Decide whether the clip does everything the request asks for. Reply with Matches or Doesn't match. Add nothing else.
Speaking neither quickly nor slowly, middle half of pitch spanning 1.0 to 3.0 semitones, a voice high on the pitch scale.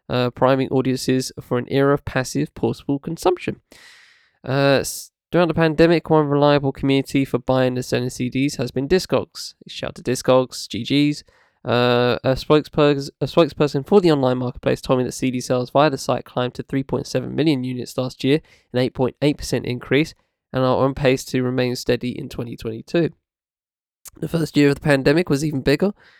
Doesn't match